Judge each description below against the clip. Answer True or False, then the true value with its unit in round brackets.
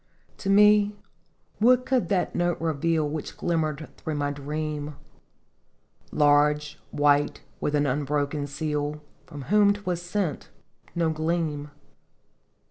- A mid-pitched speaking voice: True (155 Hz)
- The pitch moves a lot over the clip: False (3.1 semitones)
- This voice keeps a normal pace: False (125 wpm)